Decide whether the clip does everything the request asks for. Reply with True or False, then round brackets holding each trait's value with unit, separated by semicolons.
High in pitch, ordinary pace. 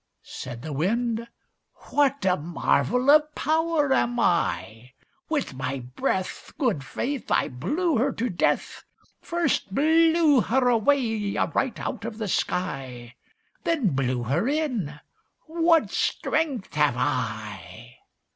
False (225 Hz; 120 wpm)